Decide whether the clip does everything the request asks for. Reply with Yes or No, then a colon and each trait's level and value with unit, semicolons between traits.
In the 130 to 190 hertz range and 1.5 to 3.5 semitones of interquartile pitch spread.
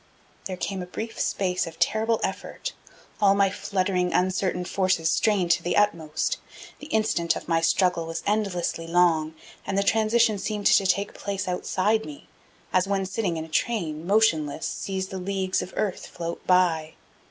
Yes: medium, 185 Hz; average, 3.0 semitones